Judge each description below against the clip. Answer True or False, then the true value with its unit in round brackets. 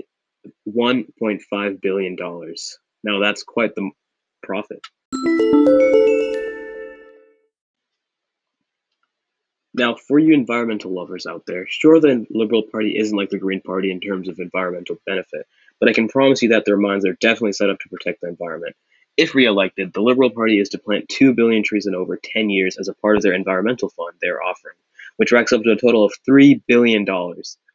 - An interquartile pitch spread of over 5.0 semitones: True (5.6 semitones)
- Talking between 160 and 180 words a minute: True (170 wpm)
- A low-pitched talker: True (110 Hz)